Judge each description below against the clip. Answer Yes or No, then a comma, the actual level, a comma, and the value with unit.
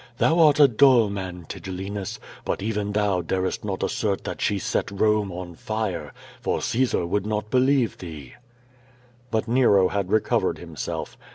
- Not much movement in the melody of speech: No, average, 3.0 semitones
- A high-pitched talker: No, low, 105 Hz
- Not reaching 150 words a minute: No, average, 155 wpm